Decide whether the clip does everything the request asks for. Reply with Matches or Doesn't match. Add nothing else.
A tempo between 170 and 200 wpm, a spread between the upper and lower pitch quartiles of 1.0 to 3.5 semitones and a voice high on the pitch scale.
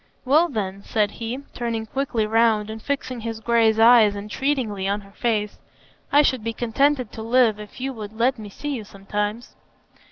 Matches